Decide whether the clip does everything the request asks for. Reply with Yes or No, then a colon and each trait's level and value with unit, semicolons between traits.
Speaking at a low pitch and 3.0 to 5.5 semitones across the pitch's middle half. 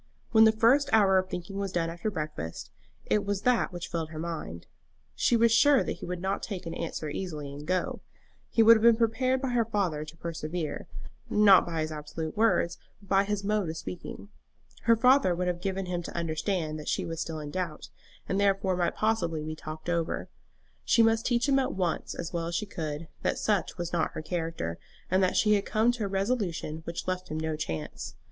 No: medium, 180 Hz; average, 4.7 semitones